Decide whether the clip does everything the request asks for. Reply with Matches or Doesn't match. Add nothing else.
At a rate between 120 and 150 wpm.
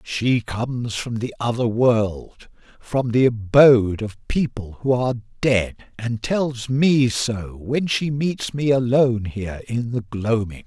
Matches